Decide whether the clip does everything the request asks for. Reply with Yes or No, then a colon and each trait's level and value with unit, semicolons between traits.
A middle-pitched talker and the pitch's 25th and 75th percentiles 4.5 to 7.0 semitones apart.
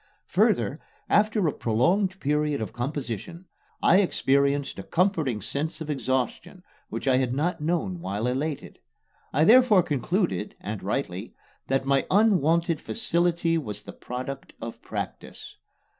Yes: medium, 150 Hz; average, 5.1 semitones